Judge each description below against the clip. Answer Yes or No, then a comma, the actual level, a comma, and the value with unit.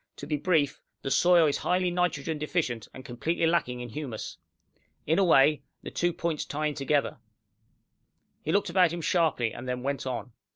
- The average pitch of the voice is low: No, medium, 150 Hz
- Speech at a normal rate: Yes, average, 180 wpm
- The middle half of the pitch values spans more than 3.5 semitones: Yes, average, 4.3 semitones